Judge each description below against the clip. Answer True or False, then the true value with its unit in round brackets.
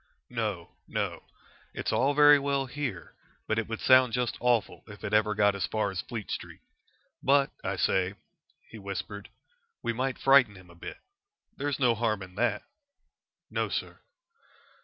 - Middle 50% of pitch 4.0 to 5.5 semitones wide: True (4.3 semitones)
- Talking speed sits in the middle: True (160 wpm)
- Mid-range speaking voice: False (115 Hz)